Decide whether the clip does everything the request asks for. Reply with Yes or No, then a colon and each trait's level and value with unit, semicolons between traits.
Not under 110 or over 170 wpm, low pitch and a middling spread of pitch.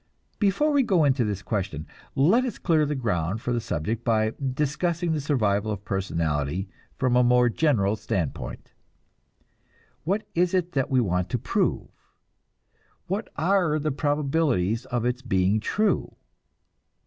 No: average, 145 wpm; low, 125 Hz; wide, 7.5 semitones